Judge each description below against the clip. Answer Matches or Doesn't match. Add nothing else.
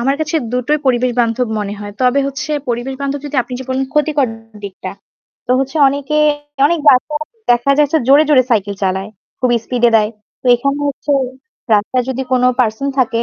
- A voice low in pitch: Doesn't match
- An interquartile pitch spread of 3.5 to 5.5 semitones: Doesn't match